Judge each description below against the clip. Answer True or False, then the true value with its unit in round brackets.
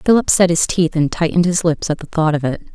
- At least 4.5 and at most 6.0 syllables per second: False (6.2 syllables/s)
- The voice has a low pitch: False (165 Hz)